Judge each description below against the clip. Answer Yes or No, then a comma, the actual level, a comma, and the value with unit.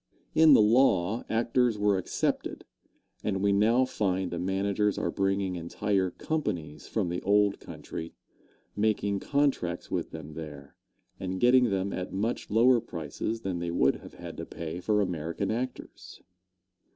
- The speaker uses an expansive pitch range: No, average, 4.0 semitones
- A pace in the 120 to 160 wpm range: Yes, average, 150 wpm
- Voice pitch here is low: Yes, low, 100 Hz